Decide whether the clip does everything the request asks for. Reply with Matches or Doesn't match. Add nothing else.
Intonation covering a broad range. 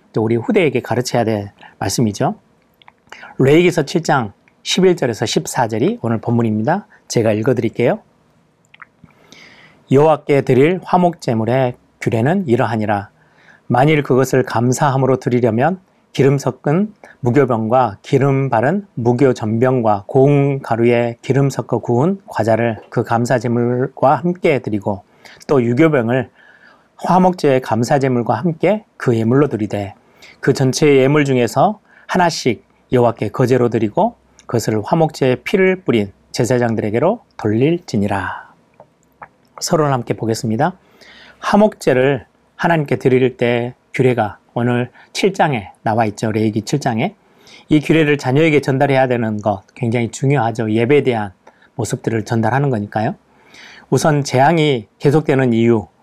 Doesn't match